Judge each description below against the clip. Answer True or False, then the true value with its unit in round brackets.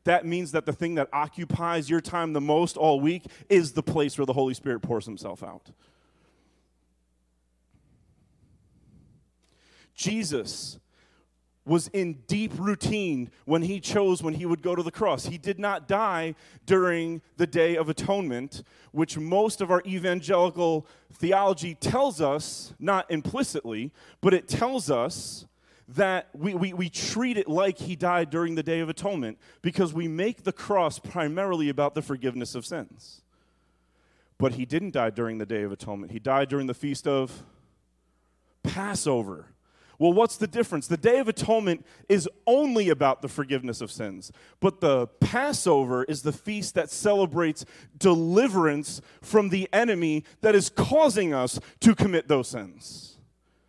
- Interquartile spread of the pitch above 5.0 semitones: True (5.5 semitones)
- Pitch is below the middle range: False (165 Hz)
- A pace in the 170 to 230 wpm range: False (155 wpm)